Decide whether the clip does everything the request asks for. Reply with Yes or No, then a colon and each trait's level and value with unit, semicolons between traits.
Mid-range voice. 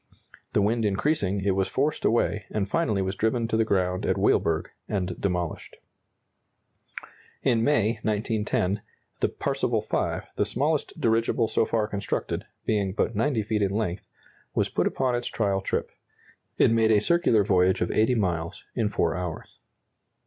No: low, 105 Hz